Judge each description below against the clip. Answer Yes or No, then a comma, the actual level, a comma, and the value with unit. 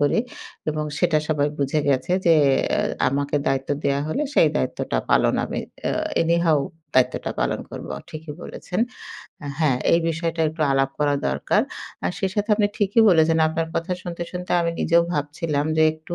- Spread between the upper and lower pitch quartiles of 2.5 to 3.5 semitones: Yes, average, 2.9 semitones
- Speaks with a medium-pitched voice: Yes, medium, 155 Hz